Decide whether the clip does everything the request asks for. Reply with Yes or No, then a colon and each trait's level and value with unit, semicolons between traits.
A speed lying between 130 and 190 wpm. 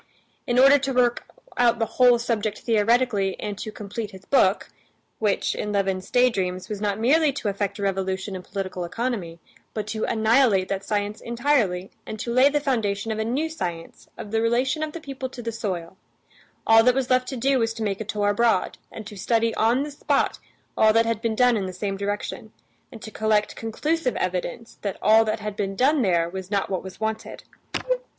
No: fast, 205 wpm